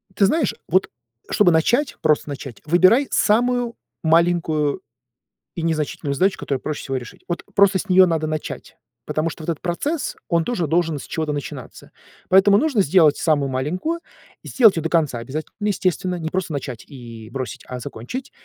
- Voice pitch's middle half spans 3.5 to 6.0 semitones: Yes, average, 4.6 semitones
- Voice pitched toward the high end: No, medium, 165 Hz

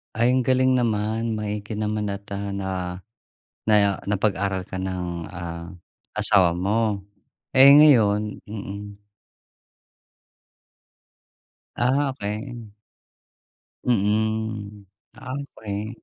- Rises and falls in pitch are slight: Yes, narrow, 2.1 semitones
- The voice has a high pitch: No, low, 105 Hz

